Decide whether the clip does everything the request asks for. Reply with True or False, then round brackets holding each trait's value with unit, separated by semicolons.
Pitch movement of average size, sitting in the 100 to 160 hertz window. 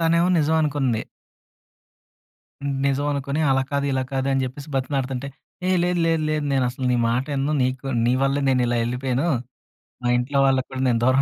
False (1.9 semitones; 135 Hz)